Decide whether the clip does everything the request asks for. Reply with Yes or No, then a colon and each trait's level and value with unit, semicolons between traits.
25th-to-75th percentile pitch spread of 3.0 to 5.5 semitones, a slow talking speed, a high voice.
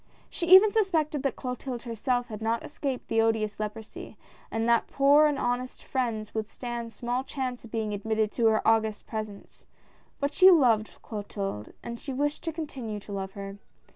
No: average, 4.1 semitones; average, 175 wpm; high, 235 Hz